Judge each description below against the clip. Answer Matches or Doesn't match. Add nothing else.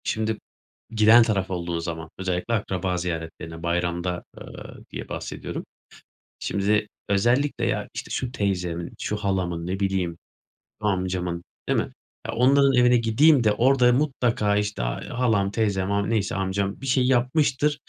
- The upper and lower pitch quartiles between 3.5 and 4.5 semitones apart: Doesn't match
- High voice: Doesn't match